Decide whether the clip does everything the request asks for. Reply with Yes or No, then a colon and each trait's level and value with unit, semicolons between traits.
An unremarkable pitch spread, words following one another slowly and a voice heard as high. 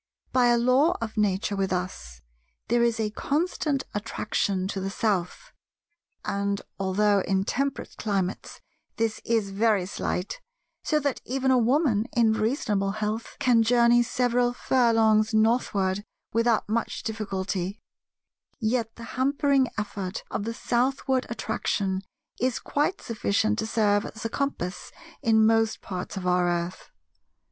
Yes: average, 3.5 semitones; slow, 130 wpm; high, 220 Hz